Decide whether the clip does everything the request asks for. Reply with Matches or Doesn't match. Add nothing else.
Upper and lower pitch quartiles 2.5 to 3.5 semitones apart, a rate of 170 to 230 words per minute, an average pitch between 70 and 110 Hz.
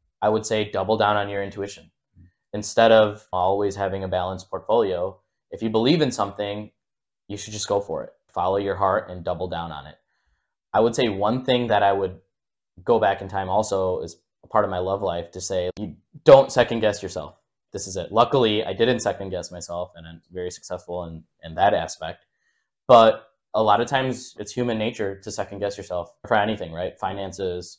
Matches